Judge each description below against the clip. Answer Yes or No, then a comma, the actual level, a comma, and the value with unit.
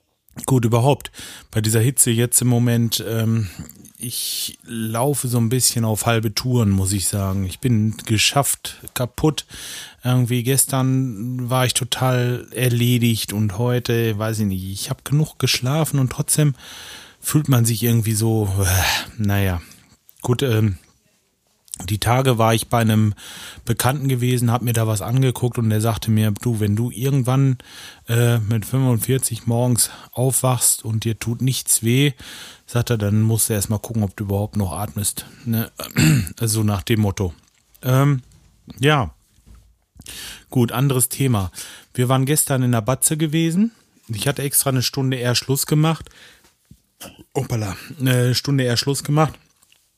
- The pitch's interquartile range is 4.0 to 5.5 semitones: No, average, 3.0 semitones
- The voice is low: Yes, low, 120 Hz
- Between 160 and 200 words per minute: No, average, 150 wpm